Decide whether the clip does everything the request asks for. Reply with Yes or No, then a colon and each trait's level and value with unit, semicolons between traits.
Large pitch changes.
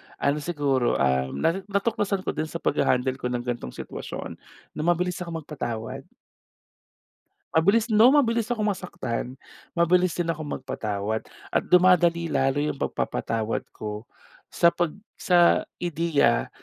Yes: wide, 6.5 semitones